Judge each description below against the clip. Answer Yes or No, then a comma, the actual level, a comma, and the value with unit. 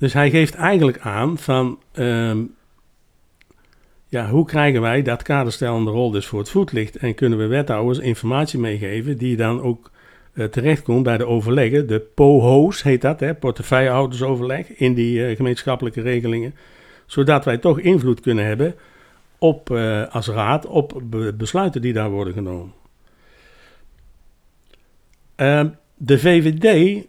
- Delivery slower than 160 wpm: Yes, slow, 135 wpm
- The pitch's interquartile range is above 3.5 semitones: Yes, average, 4.0 semitones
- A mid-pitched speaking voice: No, low, 125 Hz